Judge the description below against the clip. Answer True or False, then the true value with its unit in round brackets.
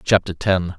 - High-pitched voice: False (95 Hz)